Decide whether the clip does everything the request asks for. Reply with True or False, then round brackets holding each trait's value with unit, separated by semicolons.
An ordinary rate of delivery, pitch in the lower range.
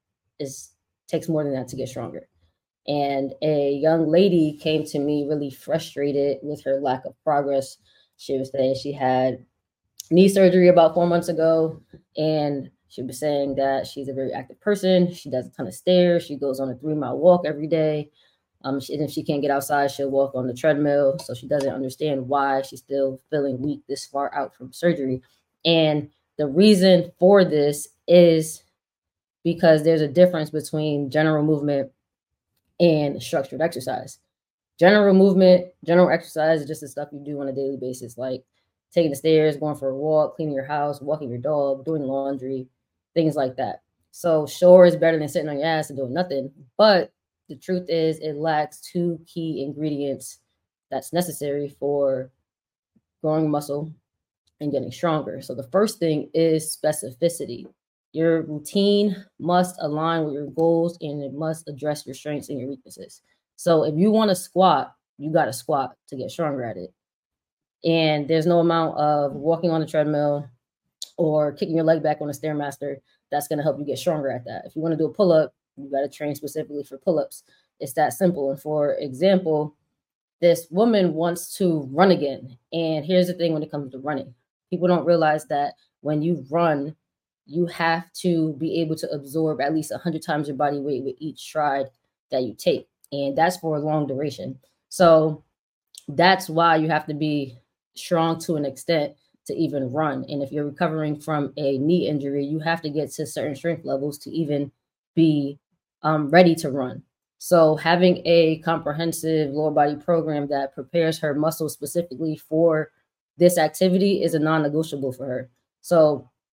False (185 wpm; 150 Hz)